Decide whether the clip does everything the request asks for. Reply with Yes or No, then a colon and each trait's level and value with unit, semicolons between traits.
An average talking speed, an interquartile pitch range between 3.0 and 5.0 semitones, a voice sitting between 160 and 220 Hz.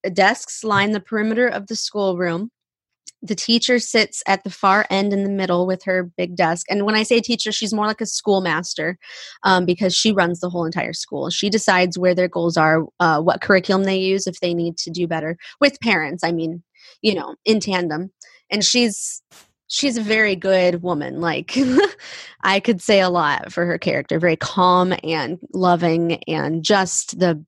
Yes: average, 190 wpm; average, 3.6 semitones; high, 190 Hz